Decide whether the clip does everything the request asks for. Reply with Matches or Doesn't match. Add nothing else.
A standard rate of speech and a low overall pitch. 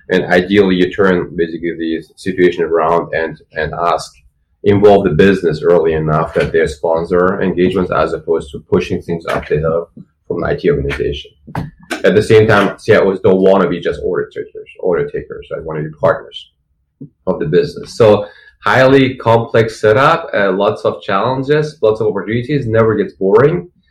Matches